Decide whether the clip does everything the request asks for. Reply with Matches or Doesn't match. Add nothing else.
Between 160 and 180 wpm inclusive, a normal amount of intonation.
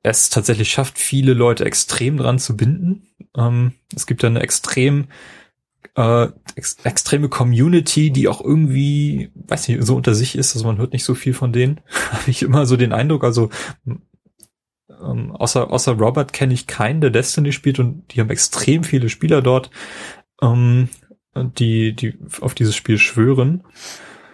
Matches